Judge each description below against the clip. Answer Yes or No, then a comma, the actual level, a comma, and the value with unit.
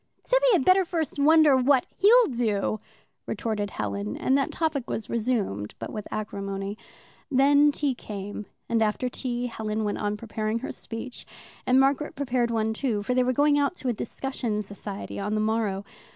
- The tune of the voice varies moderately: Yes, average, 4.7 semitones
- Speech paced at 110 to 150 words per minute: No, average, 175 wpm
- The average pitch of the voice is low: No, high, 235 Hz